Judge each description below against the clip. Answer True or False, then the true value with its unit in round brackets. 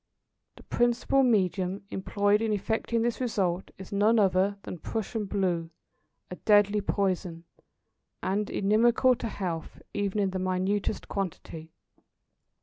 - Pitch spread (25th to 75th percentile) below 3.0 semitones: True (2.6 semitones)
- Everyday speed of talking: False (125 wpm)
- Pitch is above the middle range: True (200 Hz)